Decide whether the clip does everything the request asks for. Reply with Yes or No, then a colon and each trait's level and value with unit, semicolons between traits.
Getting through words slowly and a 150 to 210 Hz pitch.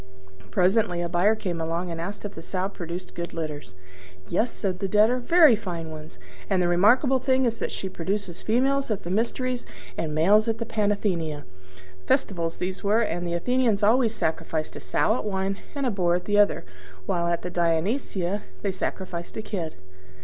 No: average, 185 wpm; high, 190 Hz